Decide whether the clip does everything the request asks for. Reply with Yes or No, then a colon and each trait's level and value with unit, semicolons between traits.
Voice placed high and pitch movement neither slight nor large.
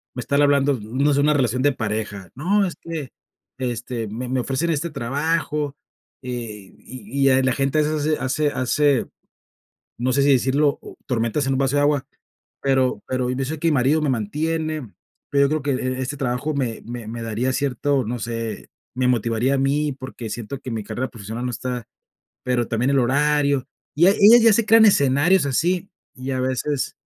No: low, 135 Hz; average, 3.1 semitones